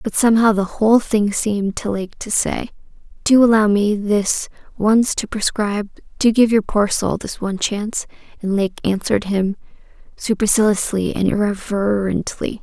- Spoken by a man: No, female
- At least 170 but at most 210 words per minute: No, average, 150 wpm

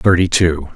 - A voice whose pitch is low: Yes, very low, 85 Hz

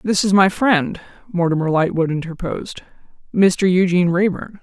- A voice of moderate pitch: Yes, medium, 180 Hz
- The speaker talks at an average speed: No, slow, 130 wpm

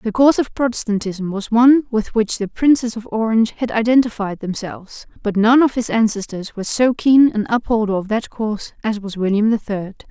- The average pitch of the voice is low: No, high, 220 Hz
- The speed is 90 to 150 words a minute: No, average, 195 wpm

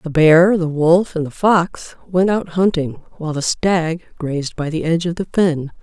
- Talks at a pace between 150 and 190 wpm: No, fast, 205 wpm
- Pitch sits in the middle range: Yes, medium, 165 Hz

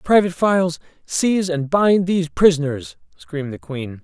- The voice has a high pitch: No, medium, 160 Hz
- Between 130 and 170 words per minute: Yes, average, 150 wpm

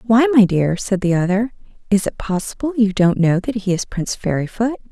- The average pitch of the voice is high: Yes, high, 210 Hz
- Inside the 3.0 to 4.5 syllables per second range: No, 5.4 syllables/s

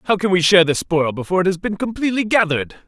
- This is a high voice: No, medium, 180 Hz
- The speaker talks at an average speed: No, fast, 250 wpm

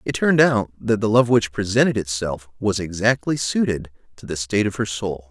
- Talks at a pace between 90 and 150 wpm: No, fast, 205 wpm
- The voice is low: Yes, low, 105 Hz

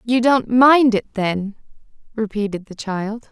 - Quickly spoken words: No, average, 145 wpm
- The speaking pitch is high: Yes, high, 220 Hz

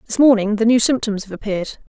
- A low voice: No, high, 220 Hz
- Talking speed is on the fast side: Yes, fast, 215 wpm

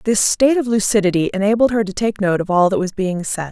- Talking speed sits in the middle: No, fast, 255 wpm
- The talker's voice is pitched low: No, high, 205 Hz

